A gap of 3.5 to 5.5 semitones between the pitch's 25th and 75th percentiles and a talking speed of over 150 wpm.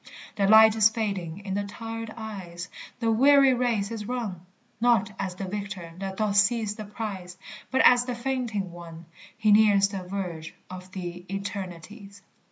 No: average, 3.1 semitones; average, 165 wpm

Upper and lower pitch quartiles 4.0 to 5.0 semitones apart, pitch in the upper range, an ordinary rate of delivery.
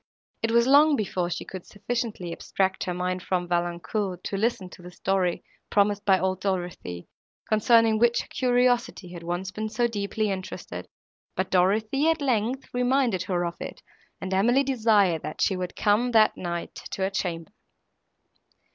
Yes: average, 4.3 semitones; high, 200 Hz; average, 165 wpm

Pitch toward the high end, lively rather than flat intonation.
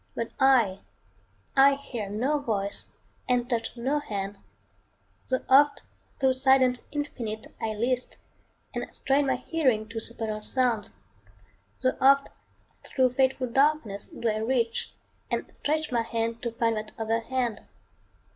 No: high, 245 Hz; average, 3.2 semitones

